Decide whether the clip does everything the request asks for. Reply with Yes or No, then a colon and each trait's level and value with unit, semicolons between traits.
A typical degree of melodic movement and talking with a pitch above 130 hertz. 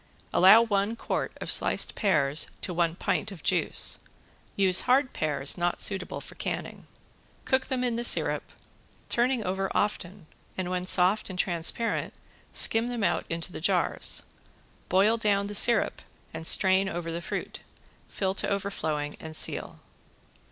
Yes: average, 3.8 semitones; high, 190 Hz